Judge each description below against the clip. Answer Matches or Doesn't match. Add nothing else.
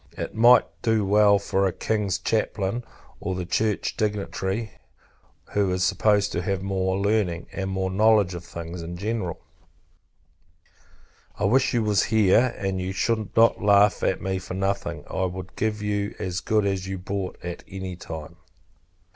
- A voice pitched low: Matches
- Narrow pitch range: Matches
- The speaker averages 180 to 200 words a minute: Doesn't match